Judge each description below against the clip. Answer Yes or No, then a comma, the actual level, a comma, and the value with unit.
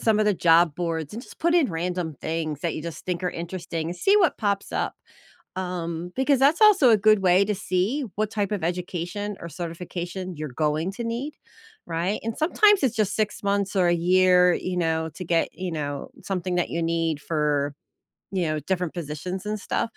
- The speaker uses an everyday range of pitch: Yes, average, 3.9 semitones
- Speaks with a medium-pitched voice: Yes, medium, 180 Hz